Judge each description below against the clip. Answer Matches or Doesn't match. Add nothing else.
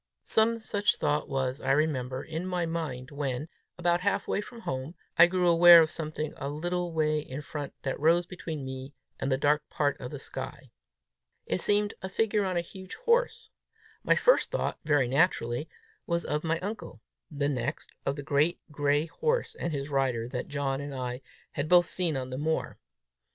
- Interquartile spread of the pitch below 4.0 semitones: Doesn't match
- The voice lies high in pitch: Doesn't match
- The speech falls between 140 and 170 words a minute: Doesn't match